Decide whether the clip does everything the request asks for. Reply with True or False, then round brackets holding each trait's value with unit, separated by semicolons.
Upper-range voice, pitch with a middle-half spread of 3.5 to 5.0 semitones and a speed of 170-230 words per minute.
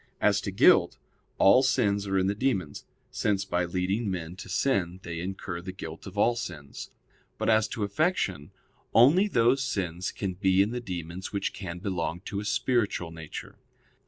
False (95 Hz; 4.0 semitones; 175 wpm)